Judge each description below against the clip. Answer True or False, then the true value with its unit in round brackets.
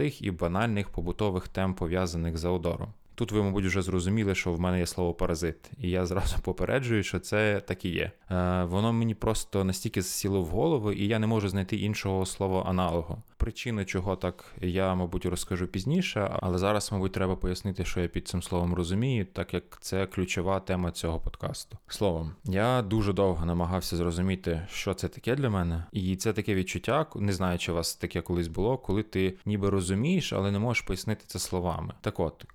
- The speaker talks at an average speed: False (190 wpm)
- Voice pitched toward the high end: False (95 Hz)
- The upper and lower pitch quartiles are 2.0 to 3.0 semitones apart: True (2.4 semitones)